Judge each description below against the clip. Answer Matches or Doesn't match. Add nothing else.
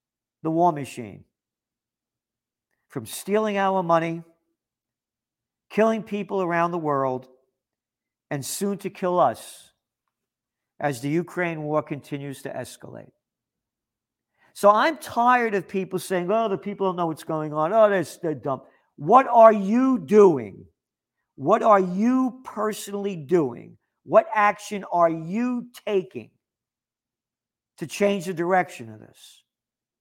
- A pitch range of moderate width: Doesn't match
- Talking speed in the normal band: Doesn't match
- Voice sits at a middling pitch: Matches